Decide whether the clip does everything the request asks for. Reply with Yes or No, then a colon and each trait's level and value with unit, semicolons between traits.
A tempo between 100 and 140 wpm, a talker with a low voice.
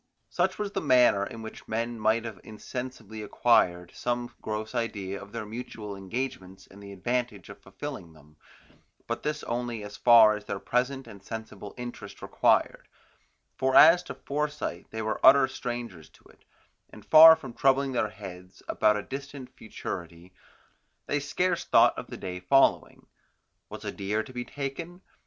No: average, 165 wpm; low, 115 Hz